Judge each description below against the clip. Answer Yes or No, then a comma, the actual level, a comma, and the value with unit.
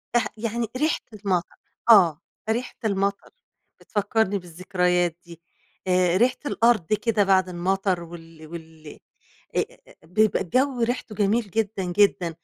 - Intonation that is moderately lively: Yes, average, 4.1 semitones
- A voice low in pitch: No, high, 195 Hz